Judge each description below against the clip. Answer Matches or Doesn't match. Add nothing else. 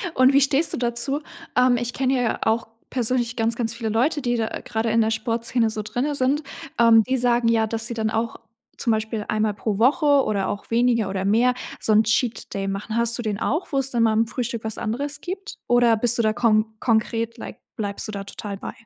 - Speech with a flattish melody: Matches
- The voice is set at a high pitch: Matches